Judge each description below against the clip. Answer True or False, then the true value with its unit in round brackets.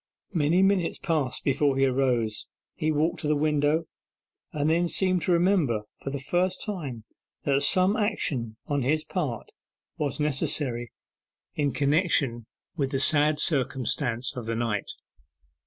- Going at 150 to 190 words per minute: False (140 wpm)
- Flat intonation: False (4.2 semitones)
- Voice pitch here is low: False (145 Hz)